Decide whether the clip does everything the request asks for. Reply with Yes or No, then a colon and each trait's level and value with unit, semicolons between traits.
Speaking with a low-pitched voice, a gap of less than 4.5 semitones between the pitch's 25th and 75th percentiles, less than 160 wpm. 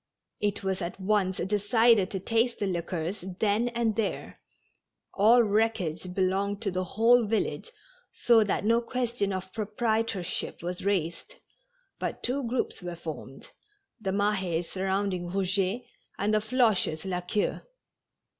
No: high, 200 Hz; average, 3.3 semitones; slow, 135 wpm